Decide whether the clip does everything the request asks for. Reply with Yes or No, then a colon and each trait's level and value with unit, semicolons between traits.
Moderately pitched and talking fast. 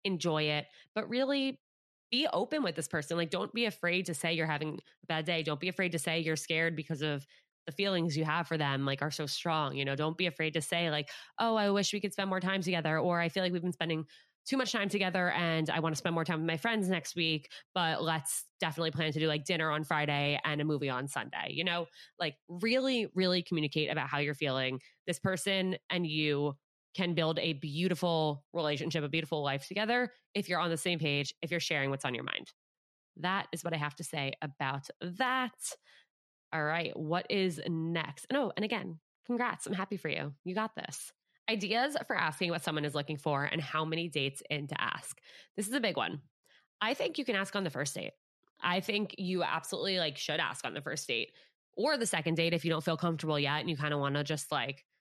Yes: medium, 165 Hz; fast, 235 wpm